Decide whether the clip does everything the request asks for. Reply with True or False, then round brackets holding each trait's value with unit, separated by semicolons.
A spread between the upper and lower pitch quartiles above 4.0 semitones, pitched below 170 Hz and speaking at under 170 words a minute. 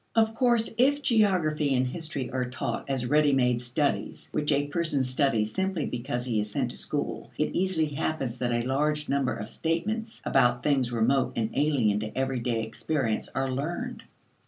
False (4.5 semitones; 140 Hz; 175 wpm)